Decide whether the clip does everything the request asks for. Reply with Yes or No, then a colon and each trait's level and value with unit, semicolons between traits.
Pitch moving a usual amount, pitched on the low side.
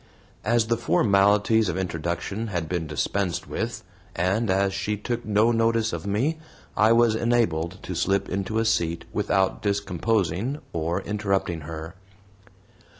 Yes: average, 4.1 semitones; low, 100 Hz